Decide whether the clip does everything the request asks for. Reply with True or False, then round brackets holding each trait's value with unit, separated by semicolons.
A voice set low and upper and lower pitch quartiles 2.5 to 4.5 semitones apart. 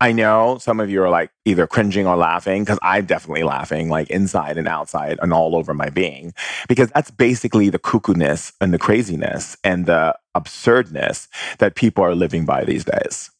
False (100 Hz; 4.9 semitones)